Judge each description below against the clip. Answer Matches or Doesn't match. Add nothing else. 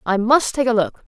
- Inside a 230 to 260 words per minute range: Matches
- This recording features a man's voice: Doesn't match